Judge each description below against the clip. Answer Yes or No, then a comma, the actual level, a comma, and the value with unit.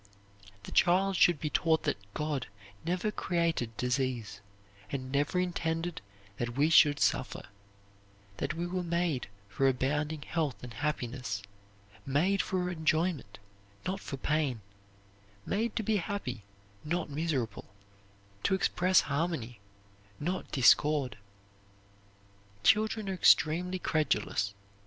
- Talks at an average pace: No, slow, 115 wpm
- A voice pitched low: No, medium, 155 Hz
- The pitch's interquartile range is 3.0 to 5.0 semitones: No, wide, 5.5 semitones